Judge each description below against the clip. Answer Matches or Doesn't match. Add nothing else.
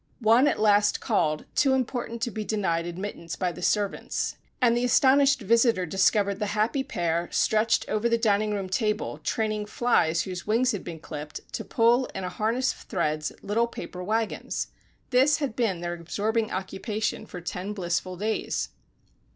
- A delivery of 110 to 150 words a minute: Doesn't match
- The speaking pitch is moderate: Doesn't match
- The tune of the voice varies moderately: Matches